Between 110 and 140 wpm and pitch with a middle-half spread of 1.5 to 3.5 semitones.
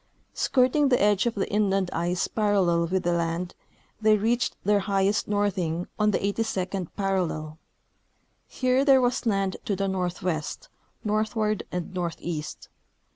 Yes: slow, 135 wpm; average, 3.2 semitones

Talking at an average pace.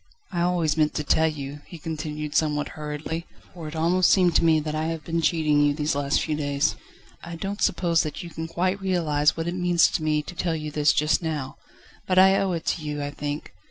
No: fast, 230 wpm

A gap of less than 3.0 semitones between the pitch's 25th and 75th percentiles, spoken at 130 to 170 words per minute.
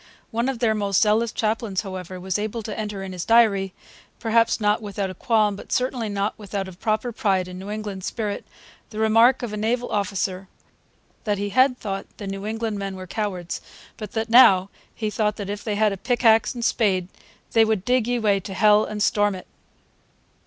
No: narrow, 2.4 semitones; fast, 205 wpm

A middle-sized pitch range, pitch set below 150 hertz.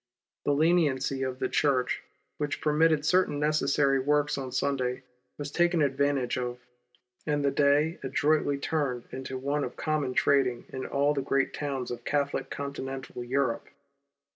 No: narrow, 2.0 semitones; medium, 140 Hz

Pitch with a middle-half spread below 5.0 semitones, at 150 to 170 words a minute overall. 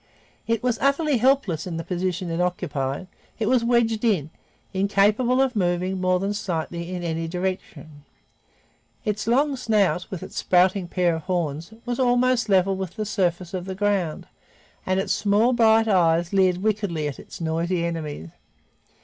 Yes: average, 4.3 semitones; average, 160 wpm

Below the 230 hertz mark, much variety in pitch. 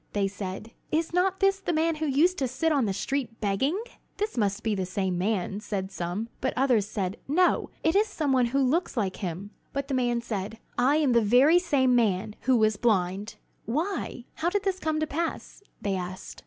No: high, 245 Hz; wide, 7.5 semitones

